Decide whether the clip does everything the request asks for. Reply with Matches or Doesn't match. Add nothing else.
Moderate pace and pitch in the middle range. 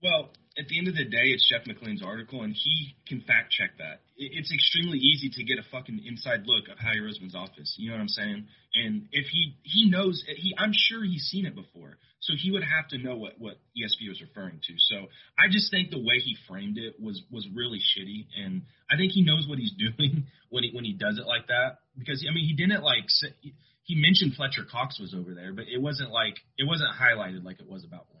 Doesn't match